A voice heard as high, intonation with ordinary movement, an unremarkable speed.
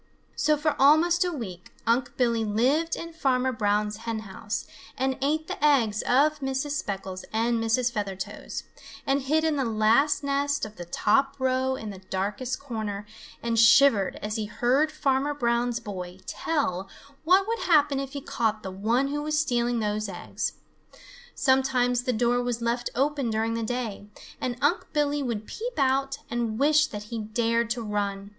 Yes: high, 245 Hz; average, 4.5 semitones; average, 170 wpm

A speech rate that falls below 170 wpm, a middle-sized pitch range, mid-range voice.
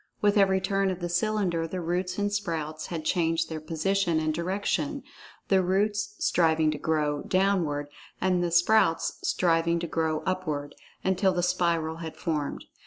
Yes: average, 150 wpm; average, 3.0 semitones; medium, 175 Hz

